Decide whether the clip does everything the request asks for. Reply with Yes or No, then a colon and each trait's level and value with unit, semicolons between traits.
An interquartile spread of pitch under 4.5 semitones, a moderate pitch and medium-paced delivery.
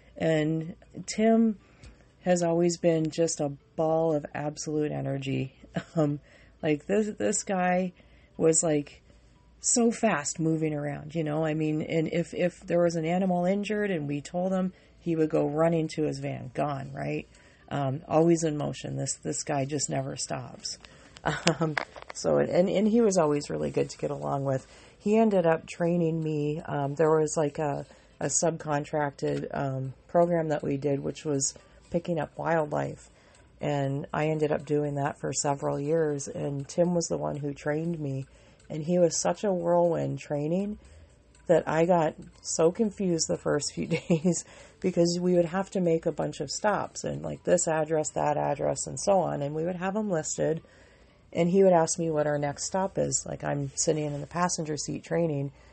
Yes: average, 3.1 semitones; medium, 155 Hz; average, 180 wpm